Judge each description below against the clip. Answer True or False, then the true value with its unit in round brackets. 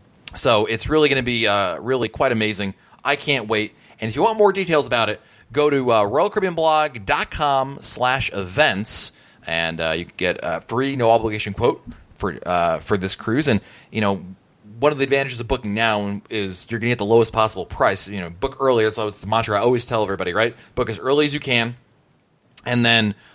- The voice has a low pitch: True (115 Hz)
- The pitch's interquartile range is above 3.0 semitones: True (4.4 semitones)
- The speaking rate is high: True (215 wpm)